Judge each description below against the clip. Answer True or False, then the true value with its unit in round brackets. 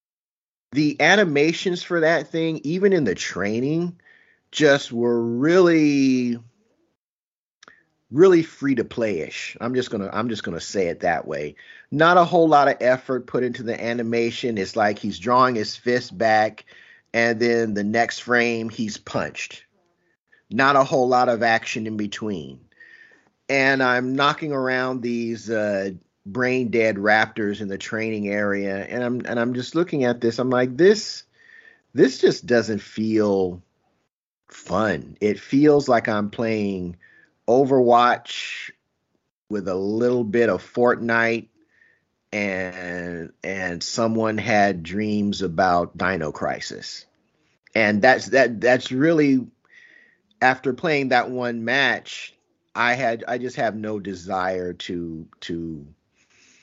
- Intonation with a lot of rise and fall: False (4.7 semitones)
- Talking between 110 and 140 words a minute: True (135 wpm)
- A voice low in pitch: True (120 Hz)